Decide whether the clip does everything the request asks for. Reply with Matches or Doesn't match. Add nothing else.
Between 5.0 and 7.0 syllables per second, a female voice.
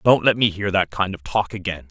Doesn't match